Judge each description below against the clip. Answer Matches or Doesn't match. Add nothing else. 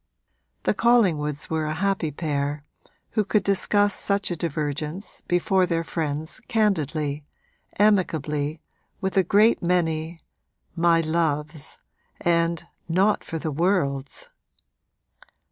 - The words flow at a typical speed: Doesn't match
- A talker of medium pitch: Matches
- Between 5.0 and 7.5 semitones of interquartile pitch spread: Doesn't match